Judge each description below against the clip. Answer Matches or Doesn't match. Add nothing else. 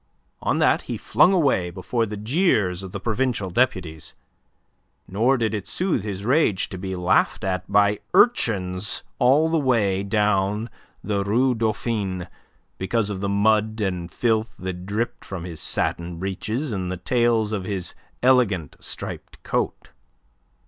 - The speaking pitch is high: Doesn't match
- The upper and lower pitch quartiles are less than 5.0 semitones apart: Matches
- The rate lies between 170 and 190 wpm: Doesn't match